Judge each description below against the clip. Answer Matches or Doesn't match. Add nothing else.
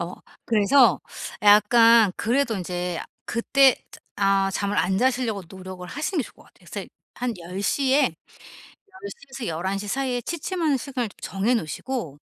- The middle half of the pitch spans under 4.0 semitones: Doesn't match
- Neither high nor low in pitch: Doesn't match